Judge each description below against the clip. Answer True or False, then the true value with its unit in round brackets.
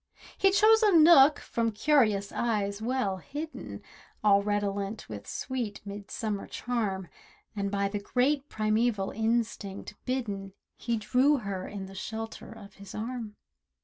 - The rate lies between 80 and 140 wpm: True (135 wpm)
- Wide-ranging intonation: False (4.0 semitones)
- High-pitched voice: True (215 Hz)